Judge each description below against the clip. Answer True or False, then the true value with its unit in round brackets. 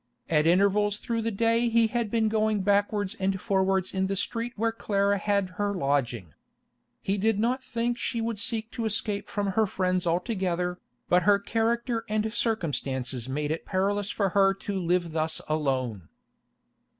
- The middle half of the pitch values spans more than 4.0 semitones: False (3.7 semitones)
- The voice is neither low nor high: False (200 Hz)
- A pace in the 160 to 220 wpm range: True (165 wpm)